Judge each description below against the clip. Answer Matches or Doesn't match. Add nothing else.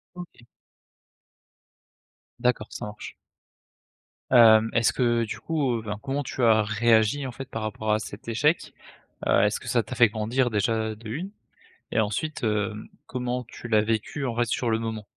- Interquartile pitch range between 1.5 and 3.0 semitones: Matches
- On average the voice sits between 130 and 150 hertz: Doesn't match